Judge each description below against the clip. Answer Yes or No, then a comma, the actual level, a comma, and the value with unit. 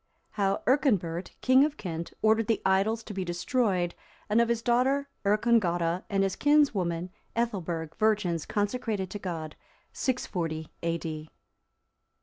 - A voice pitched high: Yes, high, 200 Hz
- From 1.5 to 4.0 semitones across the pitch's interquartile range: No, average, 5.3 semitones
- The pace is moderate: No, slow, 130 wpm